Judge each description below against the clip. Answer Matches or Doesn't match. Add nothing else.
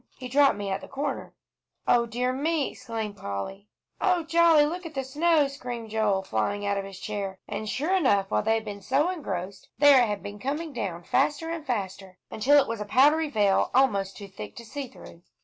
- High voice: Matches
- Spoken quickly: Matches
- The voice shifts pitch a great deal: Matches